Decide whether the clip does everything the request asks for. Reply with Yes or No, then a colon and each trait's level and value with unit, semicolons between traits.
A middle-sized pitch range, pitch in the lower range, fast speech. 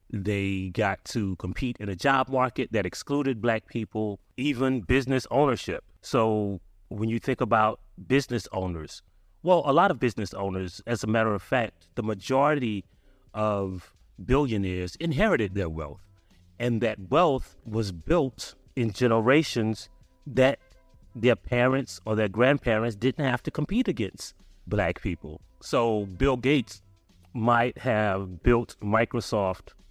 No: average, 4.6 semitones; low, 110 Hz; slow, 135 wpm